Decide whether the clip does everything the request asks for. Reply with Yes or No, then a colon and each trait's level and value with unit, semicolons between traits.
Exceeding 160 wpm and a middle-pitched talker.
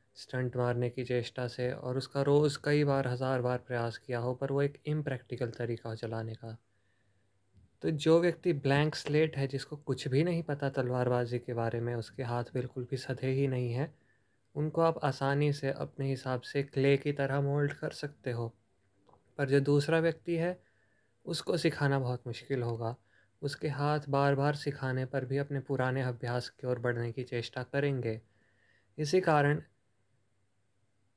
No: average, 170 wpm; low, 130 Hz